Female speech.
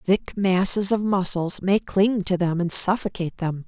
Yes: female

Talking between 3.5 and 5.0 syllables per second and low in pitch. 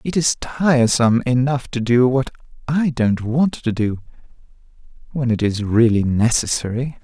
Yes: 4.6 syllables/s; low, 125 Hz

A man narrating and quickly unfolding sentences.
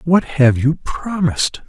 No: male; average, 145 wpm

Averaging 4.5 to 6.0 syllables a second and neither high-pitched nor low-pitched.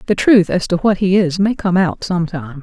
Yes: 4.9 syllables/s; medium, 180 Hz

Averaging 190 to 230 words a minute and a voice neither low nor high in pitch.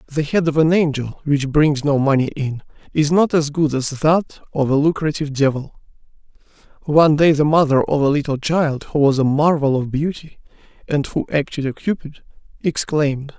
No: average, 180 wpm; medium, 145 Hz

